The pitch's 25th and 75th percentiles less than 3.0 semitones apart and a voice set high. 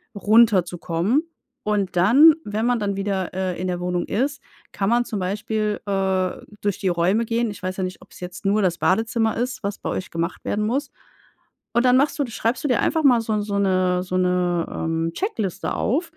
No: average, 4.0 semitones; high, 200 Hz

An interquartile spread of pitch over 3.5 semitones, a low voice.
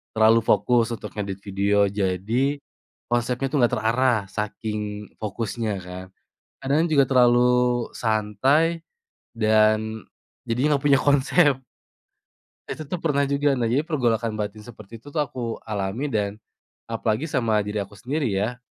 Yes: average, 4.1 semitones; low, 115 Hz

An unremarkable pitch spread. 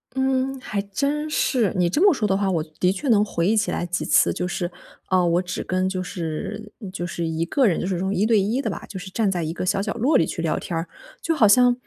Yes: average, 4.5 semitones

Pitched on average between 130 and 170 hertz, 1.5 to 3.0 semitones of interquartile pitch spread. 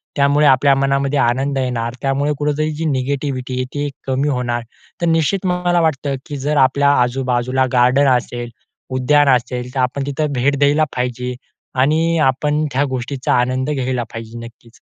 Yes: low, 135 Hz; narrow, 2.6 semitones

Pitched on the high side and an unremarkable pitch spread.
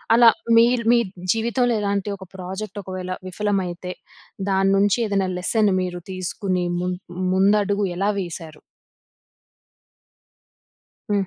No: high, 195 Hz; narrow, 2.1 semitones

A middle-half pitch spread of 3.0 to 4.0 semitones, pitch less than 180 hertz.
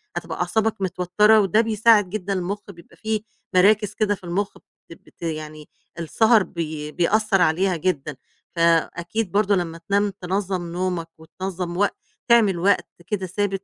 No: average, 3.4 semitones; high, 190 Hz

